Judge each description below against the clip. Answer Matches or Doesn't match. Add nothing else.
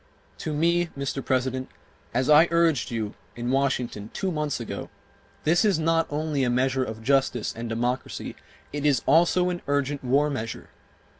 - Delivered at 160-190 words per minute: Matches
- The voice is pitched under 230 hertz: Matches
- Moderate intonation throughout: Matches